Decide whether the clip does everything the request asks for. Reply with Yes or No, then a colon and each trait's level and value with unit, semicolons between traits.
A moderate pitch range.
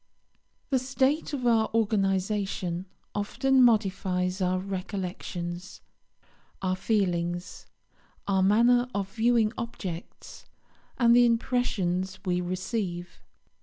Yes: average, 4.2 semitones